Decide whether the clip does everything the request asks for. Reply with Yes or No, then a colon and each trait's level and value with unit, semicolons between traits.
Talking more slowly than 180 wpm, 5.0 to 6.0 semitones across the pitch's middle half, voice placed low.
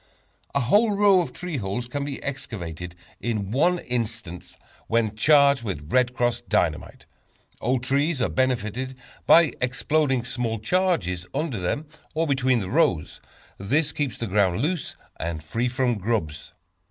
Yes: average, 145 wpm; wide, 5.6 semitones; low, 125 Hz